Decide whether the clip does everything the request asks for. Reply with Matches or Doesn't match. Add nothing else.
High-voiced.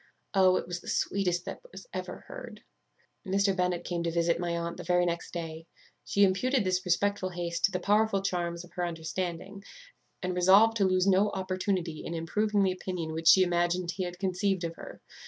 Doesn't match